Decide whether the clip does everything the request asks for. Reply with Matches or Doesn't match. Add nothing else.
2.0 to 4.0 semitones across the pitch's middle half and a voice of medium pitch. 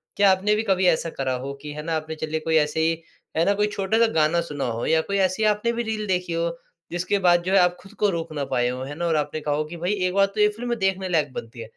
Doesn't match